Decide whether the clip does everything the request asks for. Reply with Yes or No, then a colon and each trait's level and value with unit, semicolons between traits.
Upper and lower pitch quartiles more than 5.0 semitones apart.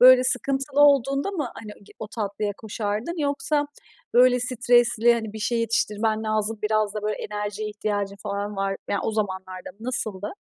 No: average, 3.3 semitones